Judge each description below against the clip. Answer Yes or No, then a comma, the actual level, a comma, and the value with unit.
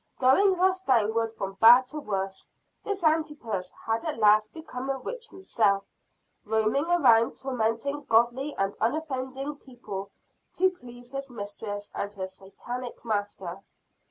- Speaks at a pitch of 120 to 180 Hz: No, high, 240 Hz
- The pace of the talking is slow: Yes, slow, 130 wpm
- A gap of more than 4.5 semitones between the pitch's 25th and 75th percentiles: Yes, wide, 5.5 semitones